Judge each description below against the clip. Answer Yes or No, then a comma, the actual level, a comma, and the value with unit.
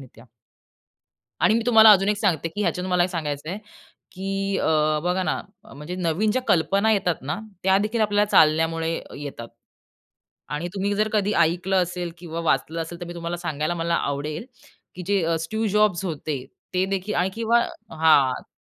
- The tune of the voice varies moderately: Yes, average, 3.8 semitones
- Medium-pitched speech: Yes, medium, 175 Hz